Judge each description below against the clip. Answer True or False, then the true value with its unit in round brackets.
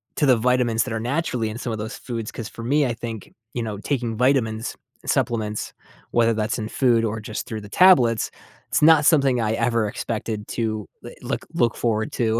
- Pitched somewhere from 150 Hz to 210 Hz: False (115 Hz)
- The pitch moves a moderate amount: False (2.2 semitones)